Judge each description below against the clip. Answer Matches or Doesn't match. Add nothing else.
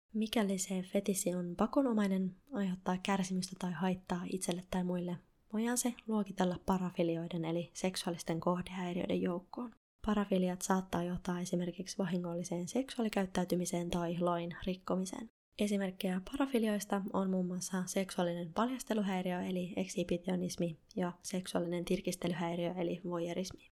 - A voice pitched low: Doesn't match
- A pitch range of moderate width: Doesn't match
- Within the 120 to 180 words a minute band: Doesn't match